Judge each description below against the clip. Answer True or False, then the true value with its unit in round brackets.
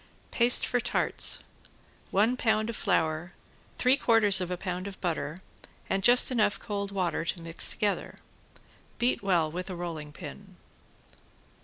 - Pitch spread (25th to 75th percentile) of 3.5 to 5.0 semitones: True (4.0 semitones)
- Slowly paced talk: False (145 wpm)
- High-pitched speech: True (195 Hz)